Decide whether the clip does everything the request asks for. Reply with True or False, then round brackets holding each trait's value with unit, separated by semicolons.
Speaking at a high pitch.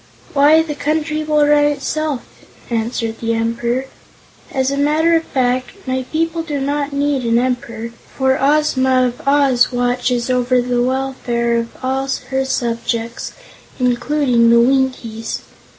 True (260 Hz)